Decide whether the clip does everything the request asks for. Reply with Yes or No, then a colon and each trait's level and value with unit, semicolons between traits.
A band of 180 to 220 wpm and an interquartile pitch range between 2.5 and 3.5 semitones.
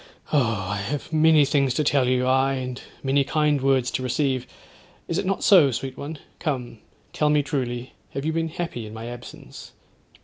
Yes: average, 190 wpm; average, 3.1 semitones